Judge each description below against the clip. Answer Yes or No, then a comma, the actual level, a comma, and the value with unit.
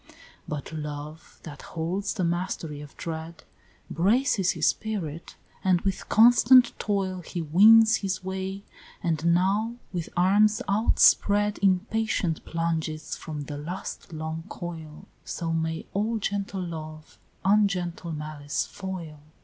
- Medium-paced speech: No, slow, 120 wpm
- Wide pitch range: No, average, 4.0 semitones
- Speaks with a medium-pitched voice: Yes, medium, 175 Hz